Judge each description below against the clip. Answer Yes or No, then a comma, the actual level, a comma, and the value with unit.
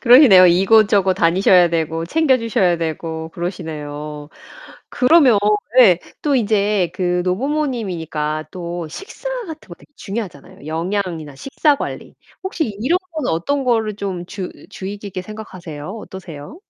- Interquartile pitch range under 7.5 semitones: Yes, wide, 5.6 semitones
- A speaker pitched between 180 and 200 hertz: Yes, high, 190 Hz